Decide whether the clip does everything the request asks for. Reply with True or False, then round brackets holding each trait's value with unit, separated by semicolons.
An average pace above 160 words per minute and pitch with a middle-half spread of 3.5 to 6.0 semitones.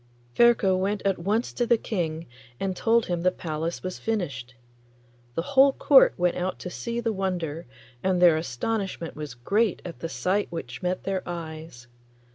True (170 wpm; 4.1 semitones)